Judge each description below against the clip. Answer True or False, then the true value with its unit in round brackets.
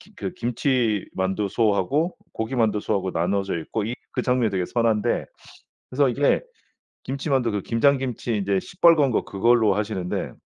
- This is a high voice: False (115 Hz)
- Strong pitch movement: False (4.5 semitones)